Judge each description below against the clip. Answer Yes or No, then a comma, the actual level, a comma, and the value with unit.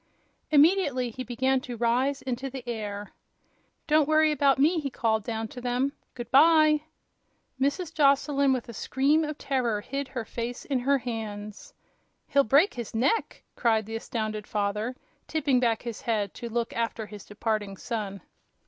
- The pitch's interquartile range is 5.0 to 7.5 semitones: No, average, 3.9 semitones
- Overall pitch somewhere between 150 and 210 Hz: No, high, 245 Hz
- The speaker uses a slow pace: No, average, 160 wpm